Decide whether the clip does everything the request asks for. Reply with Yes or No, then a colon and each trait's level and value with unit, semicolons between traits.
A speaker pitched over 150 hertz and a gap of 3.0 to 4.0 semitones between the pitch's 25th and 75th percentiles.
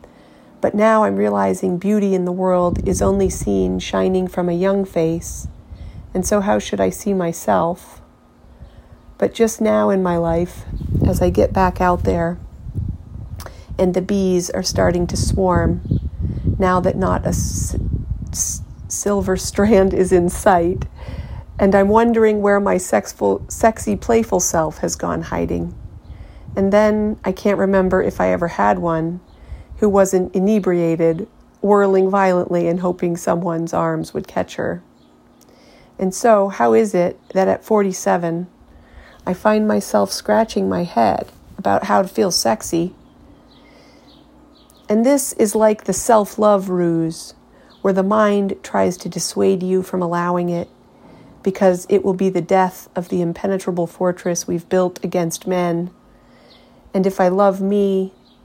Yes: medium, 185 Hz; average, 3.3 semitones